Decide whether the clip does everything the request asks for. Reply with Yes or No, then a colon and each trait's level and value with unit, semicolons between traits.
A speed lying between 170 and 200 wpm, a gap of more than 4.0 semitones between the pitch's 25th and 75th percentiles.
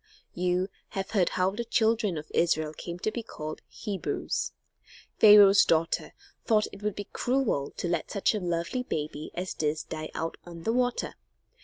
Yes: average, 175 wpm; average, 4.5 semitones